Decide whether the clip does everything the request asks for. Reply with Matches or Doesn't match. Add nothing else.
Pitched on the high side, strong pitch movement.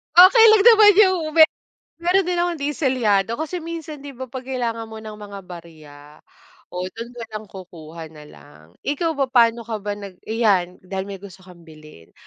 Matches